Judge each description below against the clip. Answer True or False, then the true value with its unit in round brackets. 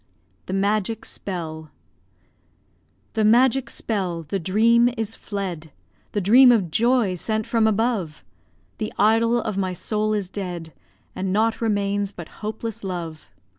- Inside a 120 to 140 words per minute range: True (135 wpm)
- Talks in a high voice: True (205 Hz)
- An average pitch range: True (3.5 semitones)